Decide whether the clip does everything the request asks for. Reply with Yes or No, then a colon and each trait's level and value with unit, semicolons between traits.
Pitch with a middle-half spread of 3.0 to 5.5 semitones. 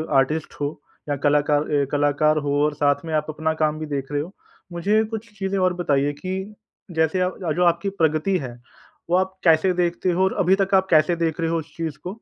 Yes: average, 3.8 semitones